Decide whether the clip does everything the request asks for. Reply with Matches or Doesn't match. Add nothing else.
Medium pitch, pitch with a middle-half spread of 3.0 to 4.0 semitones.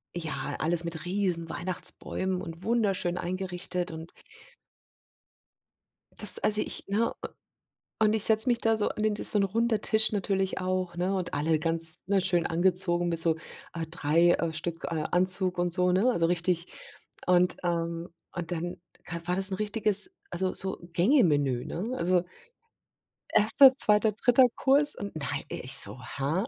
Matches